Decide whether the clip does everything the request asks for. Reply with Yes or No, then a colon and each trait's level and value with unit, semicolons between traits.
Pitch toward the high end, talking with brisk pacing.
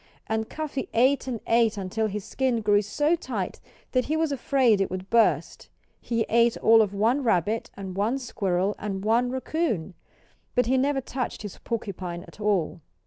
No: high, 225 Hz; average, 175 wpm